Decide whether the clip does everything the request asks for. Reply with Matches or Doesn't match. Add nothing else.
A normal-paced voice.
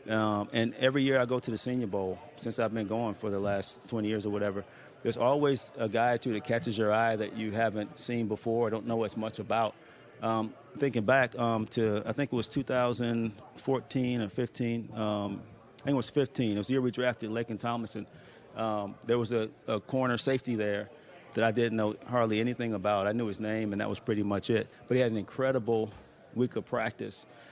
Doesn't match